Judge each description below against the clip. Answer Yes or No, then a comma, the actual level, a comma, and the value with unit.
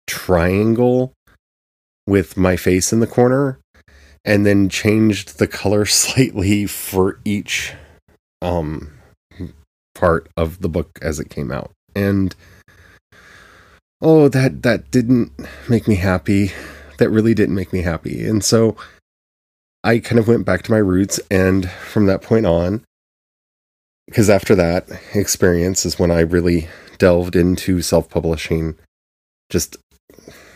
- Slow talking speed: Yes, slow, 130 wpm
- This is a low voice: Yes, very low, 90 Hz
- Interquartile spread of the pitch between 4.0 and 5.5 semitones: Yes, average, 4.3 semitones